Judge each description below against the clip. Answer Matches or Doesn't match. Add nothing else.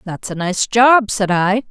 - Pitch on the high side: Matches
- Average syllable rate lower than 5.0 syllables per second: Matches